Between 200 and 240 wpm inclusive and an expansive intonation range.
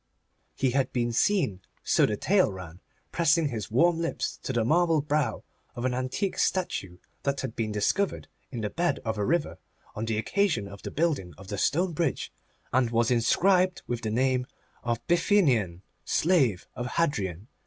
No: average, 175 wpm; wide, 7.3 semitones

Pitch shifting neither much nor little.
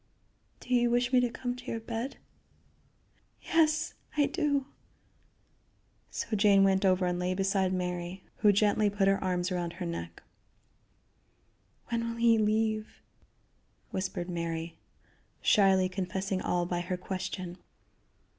Yes: average, 4.2 semitones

